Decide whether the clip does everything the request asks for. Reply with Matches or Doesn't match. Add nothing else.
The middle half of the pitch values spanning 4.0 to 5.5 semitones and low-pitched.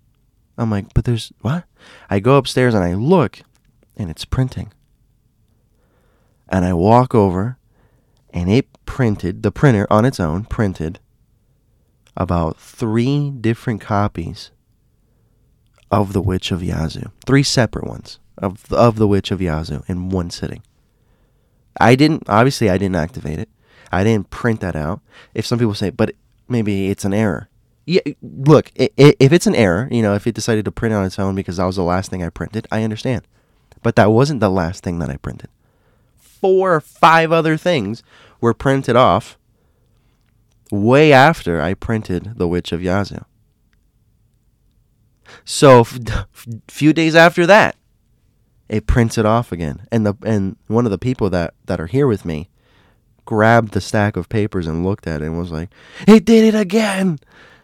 Matches